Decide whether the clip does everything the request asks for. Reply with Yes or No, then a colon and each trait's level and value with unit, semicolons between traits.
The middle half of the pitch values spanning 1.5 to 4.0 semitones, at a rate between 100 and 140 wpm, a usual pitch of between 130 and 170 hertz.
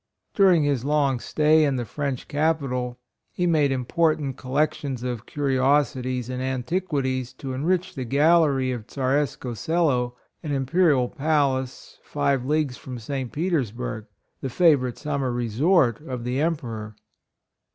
Yes: average, 3.3 semitones; slow, 135 wpm; low, 135 Hz